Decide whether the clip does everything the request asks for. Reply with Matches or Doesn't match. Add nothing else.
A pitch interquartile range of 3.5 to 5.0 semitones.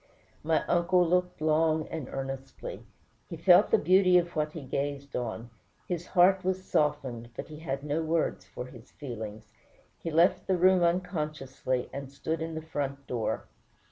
Matches